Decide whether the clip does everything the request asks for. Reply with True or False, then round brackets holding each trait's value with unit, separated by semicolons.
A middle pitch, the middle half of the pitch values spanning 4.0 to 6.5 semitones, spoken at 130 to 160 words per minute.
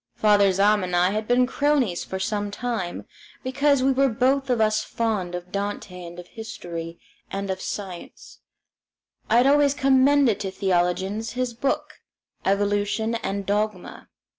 False (210 Hz; 4.7 semitones; 150 wpm)